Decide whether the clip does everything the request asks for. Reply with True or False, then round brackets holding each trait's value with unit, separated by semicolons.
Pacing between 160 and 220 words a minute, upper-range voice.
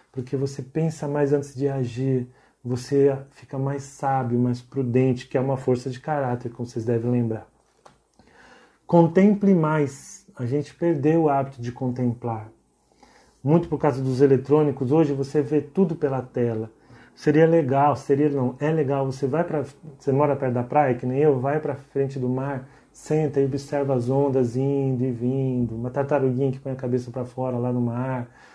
False (180 wpm; 135 Hz)